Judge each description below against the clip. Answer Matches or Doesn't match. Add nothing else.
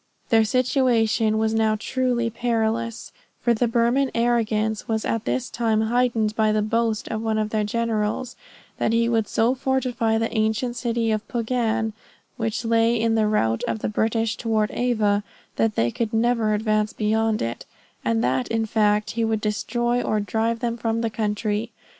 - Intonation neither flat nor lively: Doesn't match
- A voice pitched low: Doesn't match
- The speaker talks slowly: Doesn't match